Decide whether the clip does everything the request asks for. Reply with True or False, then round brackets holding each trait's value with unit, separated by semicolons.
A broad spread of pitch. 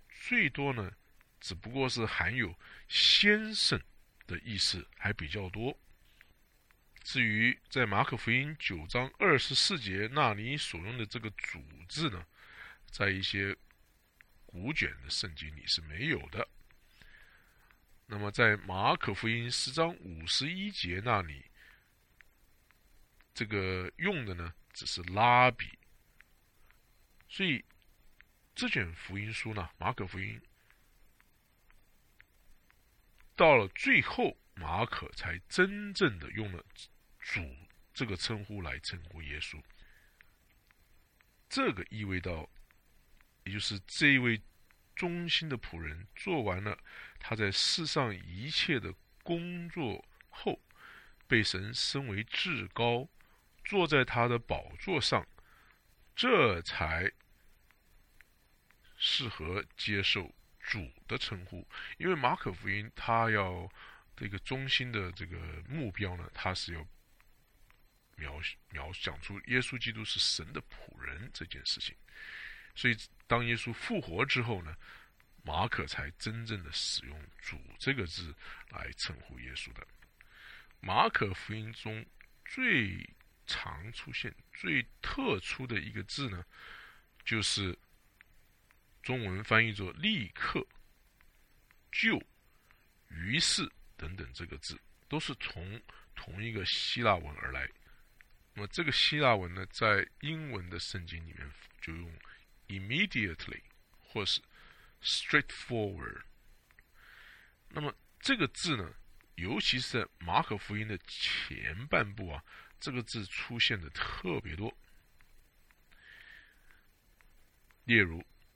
True (5.7 semitones)